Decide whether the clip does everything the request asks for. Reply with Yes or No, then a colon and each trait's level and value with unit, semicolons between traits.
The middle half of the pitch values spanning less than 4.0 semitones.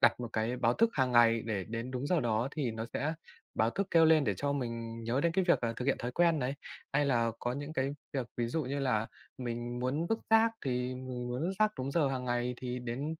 Yes: average, 3.4 semitones